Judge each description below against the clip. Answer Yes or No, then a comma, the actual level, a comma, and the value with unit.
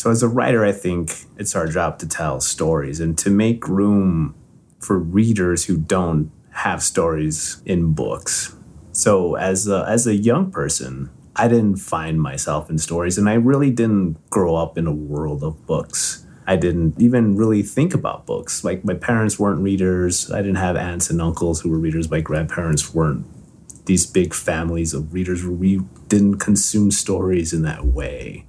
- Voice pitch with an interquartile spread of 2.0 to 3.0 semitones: No, average, 4.2 semitones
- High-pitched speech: No, very low, 90 Hz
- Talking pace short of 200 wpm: Yes, average, 175 wpm